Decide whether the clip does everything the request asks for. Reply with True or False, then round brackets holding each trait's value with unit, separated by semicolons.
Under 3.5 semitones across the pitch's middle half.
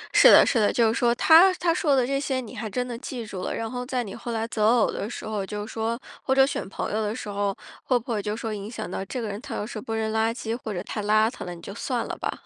True (2.9 semitones)